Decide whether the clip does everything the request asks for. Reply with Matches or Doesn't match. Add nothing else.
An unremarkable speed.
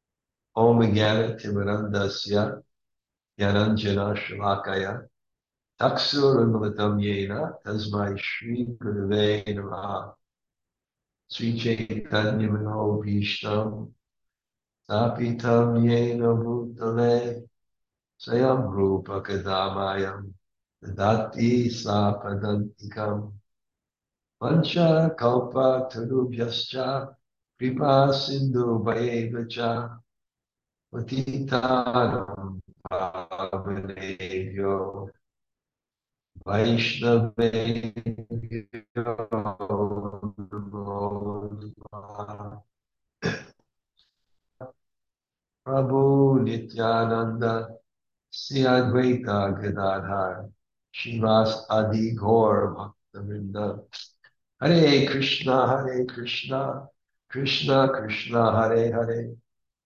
Doesn't match